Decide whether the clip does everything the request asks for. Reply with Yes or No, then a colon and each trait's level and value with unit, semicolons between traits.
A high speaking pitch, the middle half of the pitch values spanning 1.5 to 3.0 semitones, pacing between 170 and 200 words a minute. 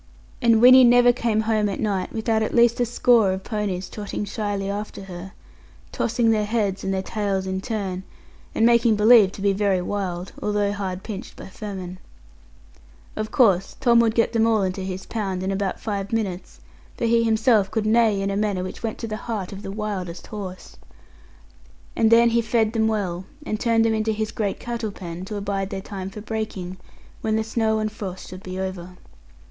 Yes: high, 210 Hz; average, 2.7 semitones; average, 195 wpm